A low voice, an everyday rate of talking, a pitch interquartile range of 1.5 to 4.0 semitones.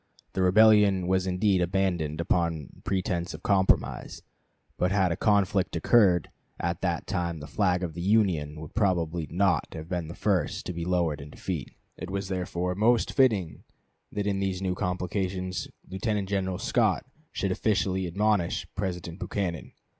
Yes: very low, 90 Hz; average, 155 wpm; narrow, 2.4 semitones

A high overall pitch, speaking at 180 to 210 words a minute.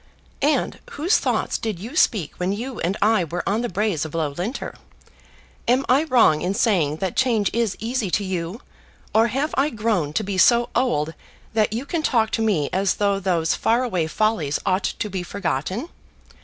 Yes: high, 210 Hz; average, 185 wpm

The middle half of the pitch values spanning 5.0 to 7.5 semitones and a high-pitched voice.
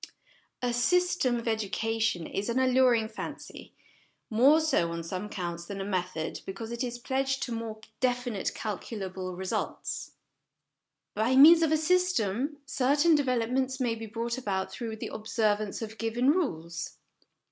No: average, 4.3 semitones; high, 230 Hz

